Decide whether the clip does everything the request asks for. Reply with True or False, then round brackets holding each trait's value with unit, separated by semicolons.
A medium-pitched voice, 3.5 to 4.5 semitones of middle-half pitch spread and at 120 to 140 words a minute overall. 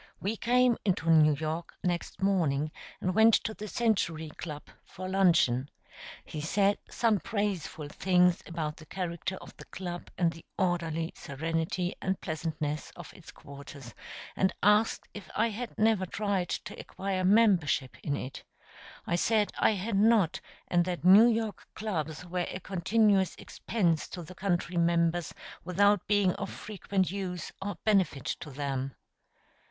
False (180 Hz; 3.9 semitones; 150 wpm)